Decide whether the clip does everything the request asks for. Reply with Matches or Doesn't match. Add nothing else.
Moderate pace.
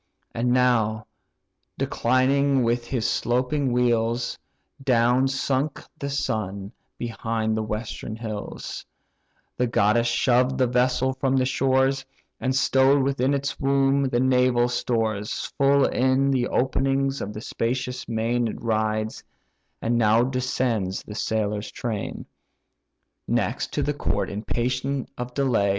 Doesn't match